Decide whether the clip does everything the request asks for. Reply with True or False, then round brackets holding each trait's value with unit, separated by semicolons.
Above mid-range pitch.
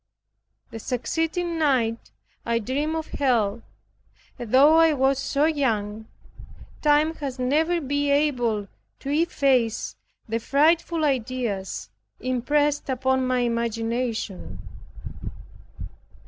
True (260 Hz)